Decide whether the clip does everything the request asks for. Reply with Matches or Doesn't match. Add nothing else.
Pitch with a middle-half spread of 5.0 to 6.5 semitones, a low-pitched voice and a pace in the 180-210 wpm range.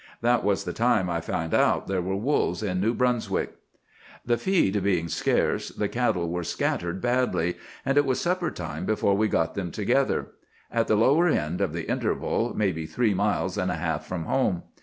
Matches